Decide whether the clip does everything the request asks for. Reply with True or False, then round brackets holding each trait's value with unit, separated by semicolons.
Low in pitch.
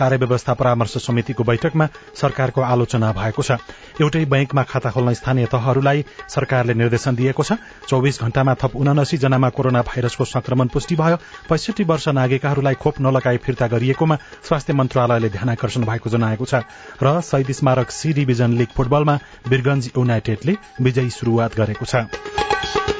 True (130 Hz)